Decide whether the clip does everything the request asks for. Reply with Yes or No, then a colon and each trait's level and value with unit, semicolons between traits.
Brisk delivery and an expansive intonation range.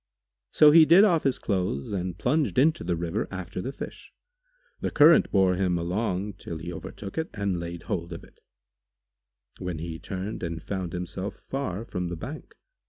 No: average, 175 wpm; wide, 6.6 semitones